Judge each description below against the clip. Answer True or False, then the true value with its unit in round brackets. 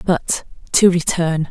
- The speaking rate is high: False (120 wpm)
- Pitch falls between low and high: True (170 Hz)